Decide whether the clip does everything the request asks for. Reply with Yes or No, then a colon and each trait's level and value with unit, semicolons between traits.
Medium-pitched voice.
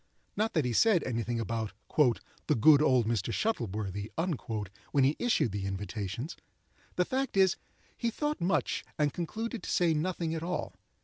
Yes: medium, 150 Hz